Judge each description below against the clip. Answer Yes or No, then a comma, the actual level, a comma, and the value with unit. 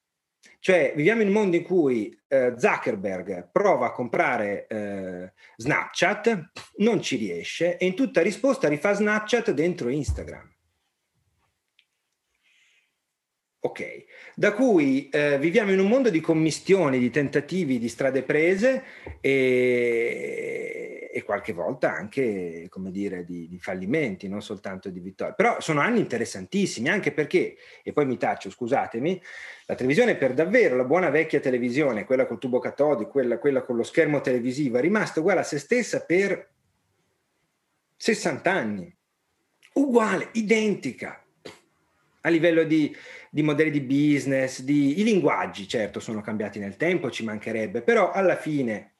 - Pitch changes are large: Yes, wide, 9.0 semitones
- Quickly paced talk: No, average, 140 wpm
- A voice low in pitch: No, medium, 160 Hz